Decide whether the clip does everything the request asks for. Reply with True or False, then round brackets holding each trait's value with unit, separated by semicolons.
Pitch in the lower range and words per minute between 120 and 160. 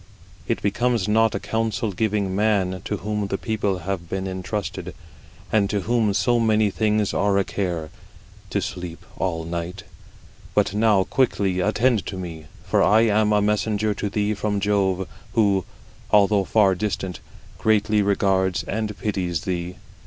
True (100 Hz; 150 wpm)